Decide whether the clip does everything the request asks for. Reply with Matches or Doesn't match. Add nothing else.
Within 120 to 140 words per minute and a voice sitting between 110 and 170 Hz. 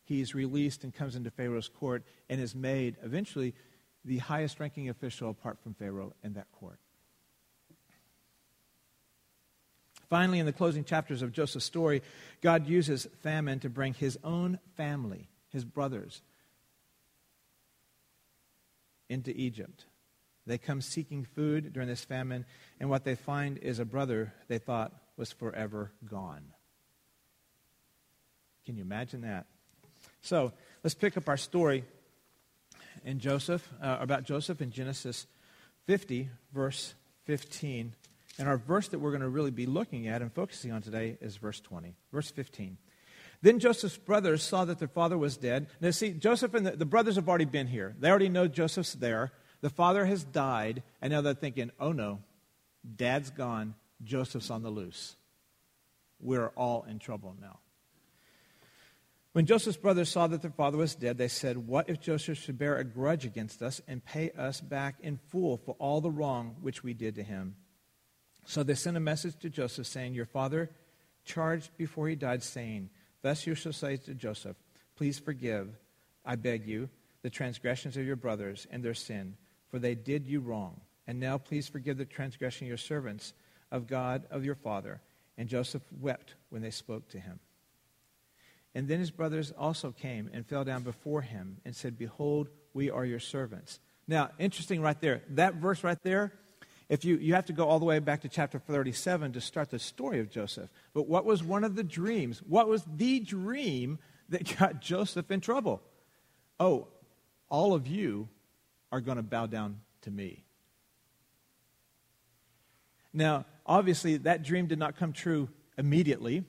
Doesn't match